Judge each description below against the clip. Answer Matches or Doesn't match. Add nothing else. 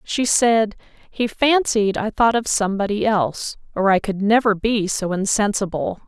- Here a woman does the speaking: Matches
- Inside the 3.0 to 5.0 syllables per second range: Matches